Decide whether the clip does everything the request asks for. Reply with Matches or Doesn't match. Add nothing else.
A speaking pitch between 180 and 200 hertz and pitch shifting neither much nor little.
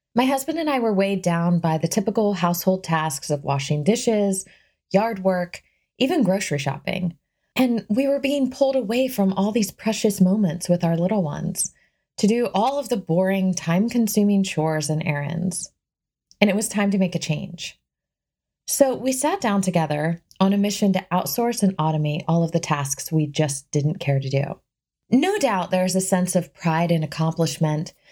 Matches